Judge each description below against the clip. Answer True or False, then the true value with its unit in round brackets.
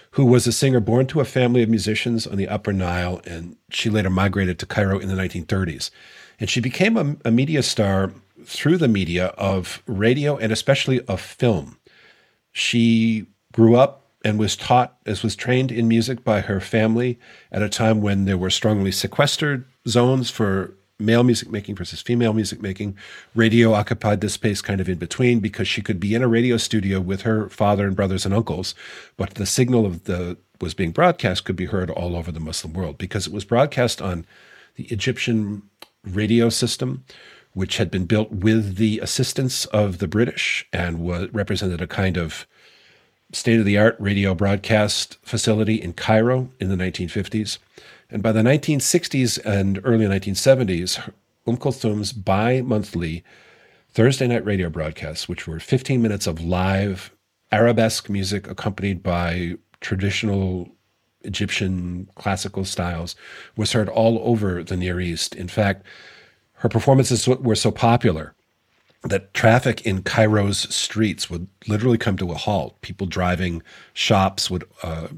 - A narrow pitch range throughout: False (3.6 semitones)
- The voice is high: False (105 Hz)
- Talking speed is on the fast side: False (160 wpm)